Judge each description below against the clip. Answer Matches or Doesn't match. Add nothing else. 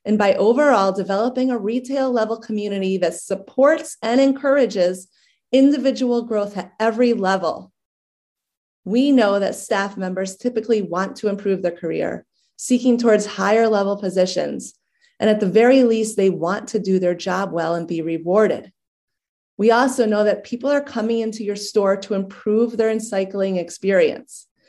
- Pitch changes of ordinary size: Matches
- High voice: Matches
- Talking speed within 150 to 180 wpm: Matches